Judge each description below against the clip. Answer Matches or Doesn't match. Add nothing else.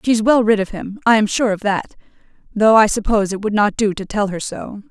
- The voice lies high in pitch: Matches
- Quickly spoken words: Matches